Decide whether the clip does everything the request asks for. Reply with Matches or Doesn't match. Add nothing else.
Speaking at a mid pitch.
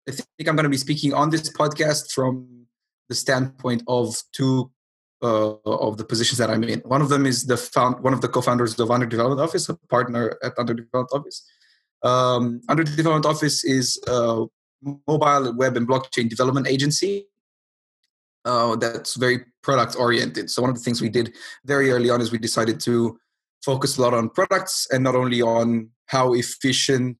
Doesn't match